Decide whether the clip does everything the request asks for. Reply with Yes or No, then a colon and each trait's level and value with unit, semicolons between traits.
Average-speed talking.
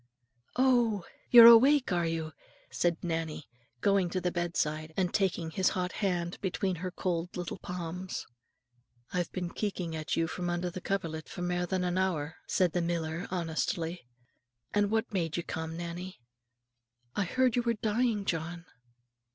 Yes: average, 160 wpm